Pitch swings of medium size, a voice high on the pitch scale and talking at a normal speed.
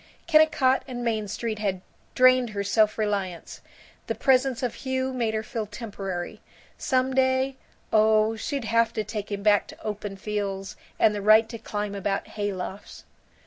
Yes: average, 3.7 semitones; high, 215 Hz; average, 165 wpm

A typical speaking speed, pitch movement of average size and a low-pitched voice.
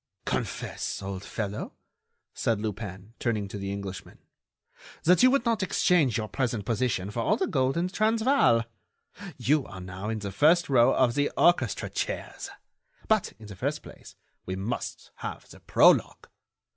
No: average, 160 wpm; wide, 7.1 semitones; low, 115 Hz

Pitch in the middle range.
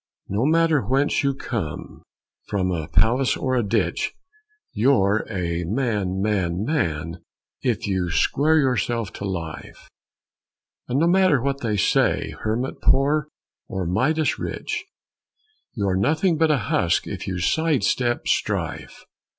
No: low, 115 Hz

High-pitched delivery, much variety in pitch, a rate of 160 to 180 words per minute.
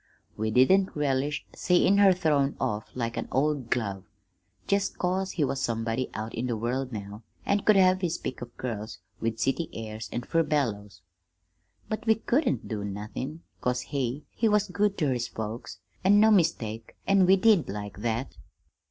No: low, 130 Hz; wide, 8.6 semitones; average, 170 wpm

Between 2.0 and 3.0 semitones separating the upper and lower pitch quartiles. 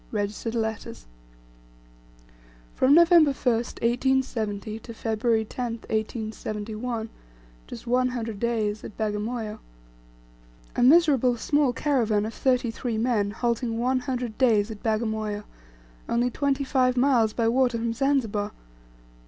Yes: narrow, 2.6 semitones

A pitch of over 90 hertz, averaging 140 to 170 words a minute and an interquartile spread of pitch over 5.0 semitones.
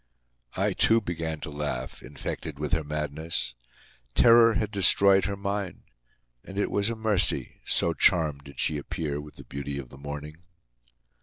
No: very low, 80 Hz; average, 160 wpm; wide, 5.4 semitones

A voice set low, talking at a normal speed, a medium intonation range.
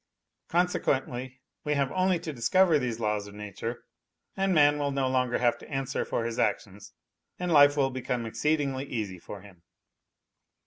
Yes: low, 130 Hz; average, 165 wpm; average, 4.5 semitones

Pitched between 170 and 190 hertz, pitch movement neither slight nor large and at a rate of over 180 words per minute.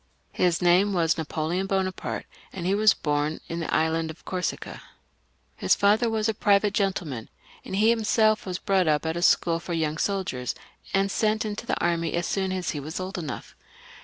Yes: medium, 185 Hz; average, 3.6 semitones; average, 190 wpm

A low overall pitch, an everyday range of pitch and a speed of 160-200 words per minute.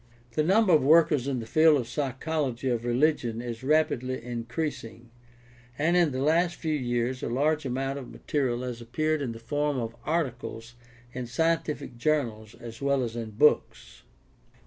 Yes: low, 130 Hz; average, 4.3 semitones; average, 165 wpm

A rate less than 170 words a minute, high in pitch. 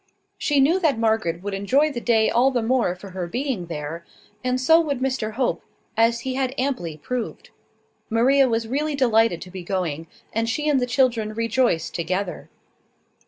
No: average, 175 wpm; high, 230 Hz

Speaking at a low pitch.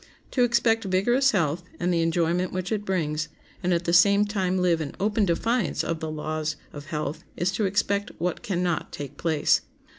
No: medium, 180 Hz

